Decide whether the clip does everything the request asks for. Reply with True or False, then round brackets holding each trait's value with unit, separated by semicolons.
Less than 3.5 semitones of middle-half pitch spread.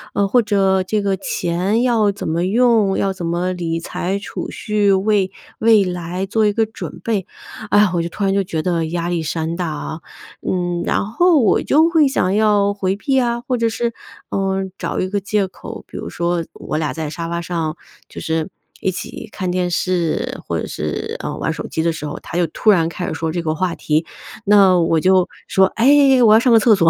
False (3.8 semitones)